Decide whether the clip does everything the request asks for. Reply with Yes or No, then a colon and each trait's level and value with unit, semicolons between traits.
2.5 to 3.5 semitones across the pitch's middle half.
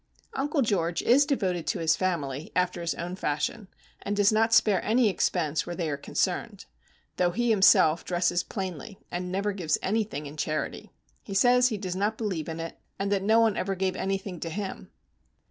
No: average, 3.9 semitones